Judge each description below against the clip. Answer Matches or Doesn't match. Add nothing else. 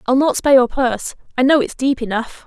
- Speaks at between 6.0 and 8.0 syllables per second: Matches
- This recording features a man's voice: Doesn't match